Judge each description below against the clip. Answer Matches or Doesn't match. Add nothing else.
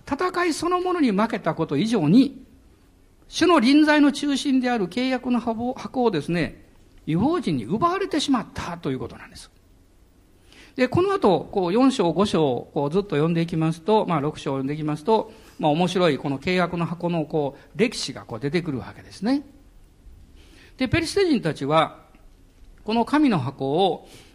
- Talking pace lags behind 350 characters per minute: Matches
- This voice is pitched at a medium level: Matches